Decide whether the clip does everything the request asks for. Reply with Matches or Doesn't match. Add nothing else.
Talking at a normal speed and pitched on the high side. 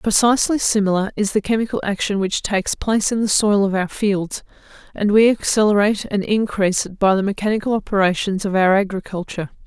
Matches